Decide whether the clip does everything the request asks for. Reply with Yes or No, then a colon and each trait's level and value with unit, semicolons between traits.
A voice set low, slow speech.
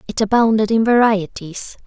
No: high, 215 Hz; slow, 130 wpm